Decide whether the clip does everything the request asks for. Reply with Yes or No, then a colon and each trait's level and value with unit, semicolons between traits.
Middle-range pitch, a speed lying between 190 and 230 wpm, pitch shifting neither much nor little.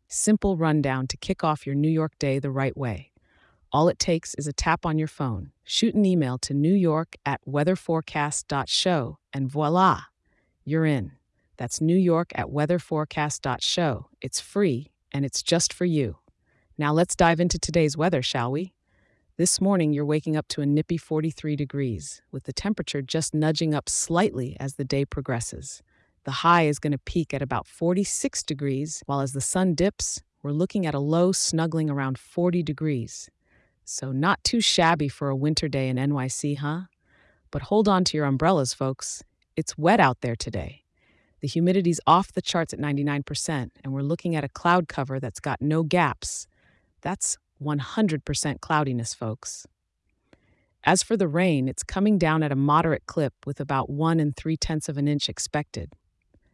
No: medium, 150 Hz; average, 170 wpm; average, 3.6 semitones